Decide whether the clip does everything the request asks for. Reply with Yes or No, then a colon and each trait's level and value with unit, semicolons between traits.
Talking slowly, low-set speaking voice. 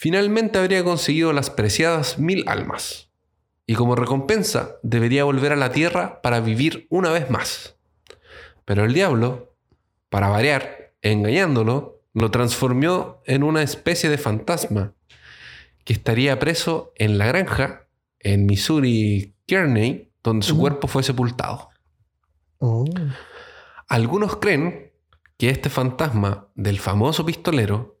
Yes: slow, 120 wpm; low, 125 Hz